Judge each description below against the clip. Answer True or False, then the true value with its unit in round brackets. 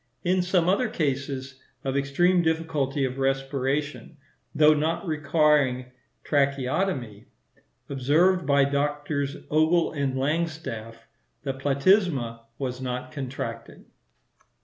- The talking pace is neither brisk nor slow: False (100 wpm)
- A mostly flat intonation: False (3.3 semitones)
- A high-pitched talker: False (140 Hz)